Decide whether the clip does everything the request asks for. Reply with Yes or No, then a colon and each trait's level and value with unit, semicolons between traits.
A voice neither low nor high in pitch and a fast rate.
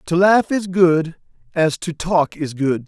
No: medium, 170 Hz; average, 190 wpm